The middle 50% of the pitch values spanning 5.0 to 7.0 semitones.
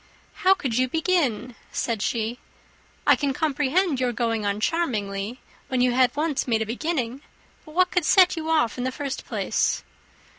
Yes: wide, 5.6 semitones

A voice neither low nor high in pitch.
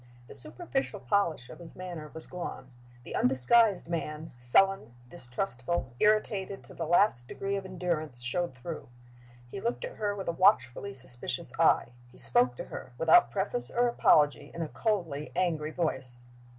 Yes: medium, 165 Hz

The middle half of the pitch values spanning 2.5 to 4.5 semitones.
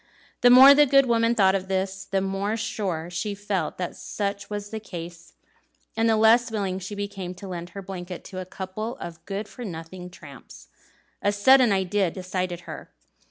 Yes: average, 2.9 semitones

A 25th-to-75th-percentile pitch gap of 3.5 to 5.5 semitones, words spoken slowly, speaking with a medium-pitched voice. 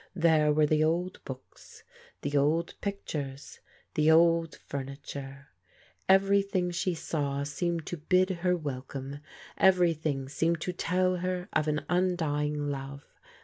Yes: average, 3.9 semitones; slow, 130 wpm; medium, 160 Hz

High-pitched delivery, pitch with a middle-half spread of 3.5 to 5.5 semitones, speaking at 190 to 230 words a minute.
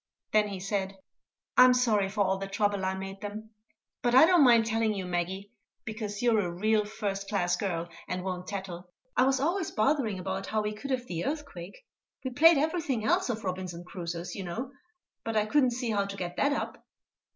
Yes: high, 210 Hz; average, 4.4 semitones; average, 200 wpm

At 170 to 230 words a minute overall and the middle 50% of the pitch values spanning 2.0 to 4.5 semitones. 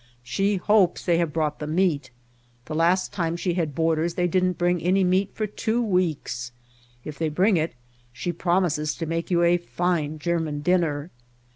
Yes: average, 180 wpm; average, 2.8 semitones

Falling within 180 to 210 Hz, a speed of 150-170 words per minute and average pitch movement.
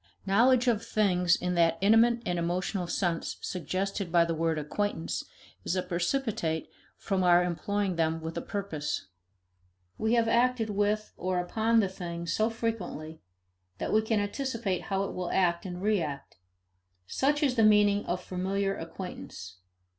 Yes: high, 190 Hz; average, 155 wpm; average, 4.0 semitones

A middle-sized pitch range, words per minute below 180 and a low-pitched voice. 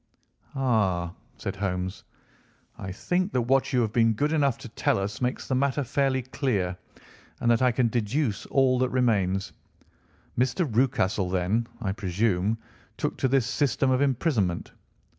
Yes: average, 5.0 semitones; average, 155 wpm; low, 120 Hz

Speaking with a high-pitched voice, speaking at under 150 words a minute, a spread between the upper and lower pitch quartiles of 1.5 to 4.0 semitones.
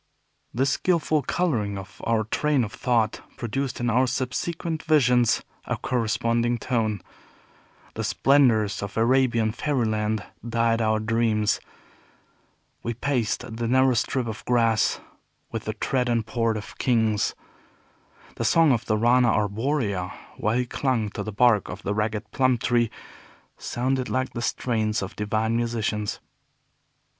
No: low, 115 Hz; slow, 135 wpm; average, 2.8 semitones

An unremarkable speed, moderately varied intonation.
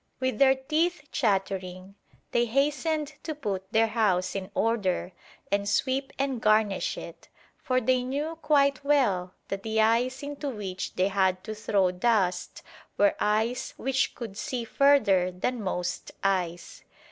No: average, 145 wpm; wide, 5.7 semitones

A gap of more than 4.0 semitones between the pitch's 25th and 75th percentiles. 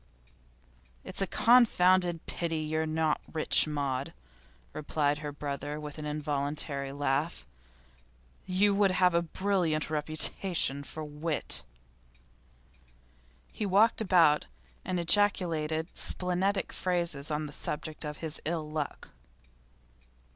No: average, 3.4 semitones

